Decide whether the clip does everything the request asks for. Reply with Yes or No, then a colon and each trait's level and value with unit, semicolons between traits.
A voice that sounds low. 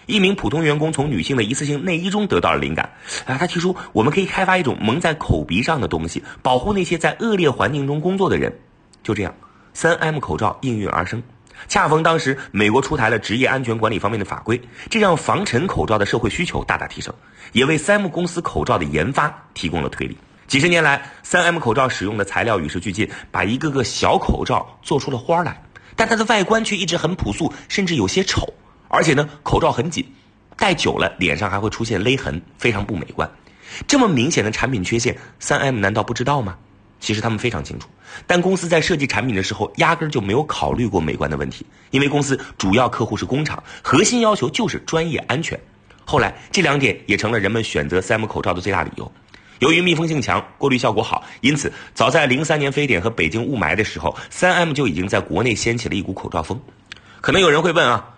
Yes: low, 125 Hz